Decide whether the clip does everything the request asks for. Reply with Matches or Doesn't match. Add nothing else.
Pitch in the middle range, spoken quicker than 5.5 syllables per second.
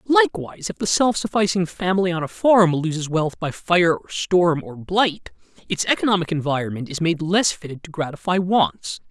Doesn't match